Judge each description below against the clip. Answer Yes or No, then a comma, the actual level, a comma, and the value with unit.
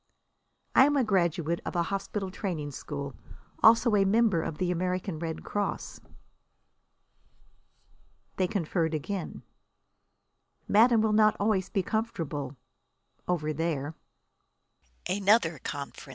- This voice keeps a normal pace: No, slow, 105 wpm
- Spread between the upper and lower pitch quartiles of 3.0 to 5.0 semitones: Yes, average, 4.6 semitones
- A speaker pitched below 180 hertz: No, medium, 185 Hz